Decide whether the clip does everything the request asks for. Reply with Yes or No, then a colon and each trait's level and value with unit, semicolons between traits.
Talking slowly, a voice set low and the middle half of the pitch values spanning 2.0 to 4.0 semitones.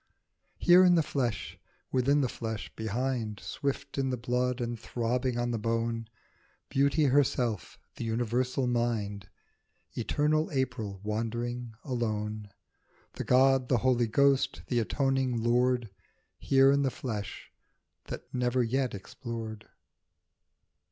Yes: slow, 120 wpm; low, 125 Hz; average, 2.7 semitones